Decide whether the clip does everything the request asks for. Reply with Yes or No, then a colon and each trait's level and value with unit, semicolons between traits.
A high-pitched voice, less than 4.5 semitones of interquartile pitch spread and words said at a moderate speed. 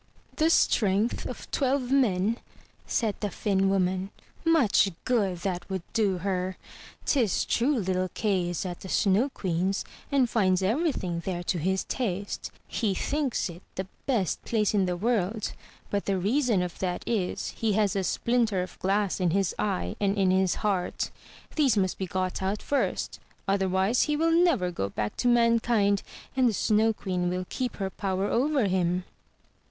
Yes: high, 195 Hz; average, 3.9 semitones; average, 170 wpm